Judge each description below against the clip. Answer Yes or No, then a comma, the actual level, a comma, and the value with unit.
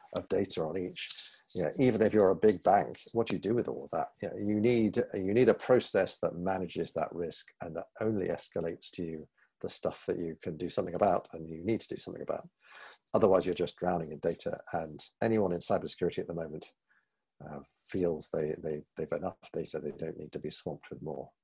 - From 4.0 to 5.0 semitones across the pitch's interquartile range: Yes, average, 4.5 semitones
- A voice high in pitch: No, low, 100 Hz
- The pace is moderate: No, fast, 225 wpm